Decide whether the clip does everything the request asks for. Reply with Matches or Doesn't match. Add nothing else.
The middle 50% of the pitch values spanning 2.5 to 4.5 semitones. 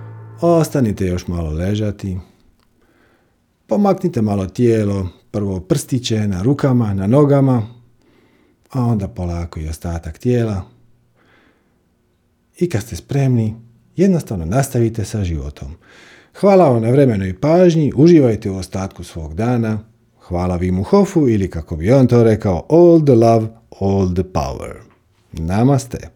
Doesn't match